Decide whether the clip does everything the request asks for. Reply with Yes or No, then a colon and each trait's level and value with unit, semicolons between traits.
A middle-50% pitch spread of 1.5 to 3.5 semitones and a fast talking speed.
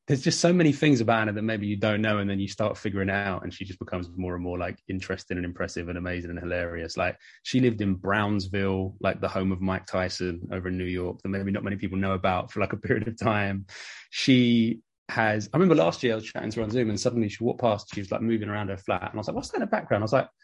Yes: average, 3.2 semitones; fast, 290 wpm